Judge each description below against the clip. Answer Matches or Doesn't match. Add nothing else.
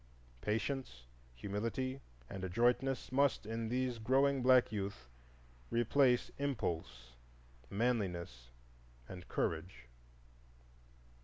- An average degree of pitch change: Doesn't match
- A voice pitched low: Matches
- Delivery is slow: Matches